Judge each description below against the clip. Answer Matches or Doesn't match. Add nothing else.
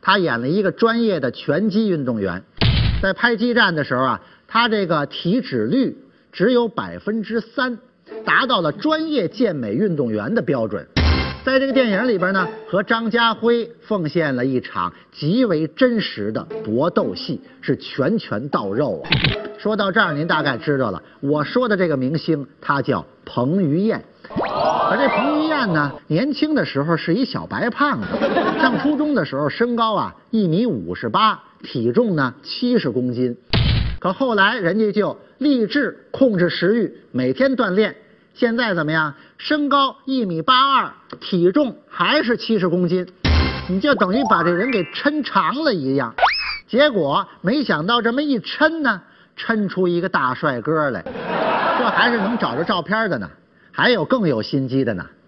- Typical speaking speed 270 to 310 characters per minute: Doesn't match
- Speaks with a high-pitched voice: Matches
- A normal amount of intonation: Doesn't match